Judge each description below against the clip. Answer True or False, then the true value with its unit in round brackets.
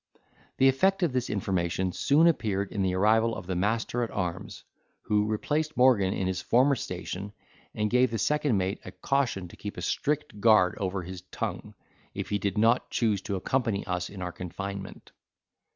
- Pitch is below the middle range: True (105 Hz)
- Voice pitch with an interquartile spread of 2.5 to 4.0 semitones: False (4.9 semitones)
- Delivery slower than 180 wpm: False (185 wpm)